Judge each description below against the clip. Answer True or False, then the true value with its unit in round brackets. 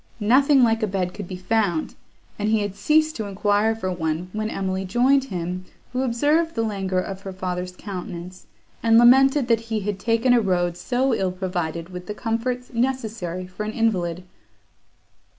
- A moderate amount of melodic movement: True (4.3 semitones)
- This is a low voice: False (210 Hz)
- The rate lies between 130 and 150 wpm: False (175 wpm)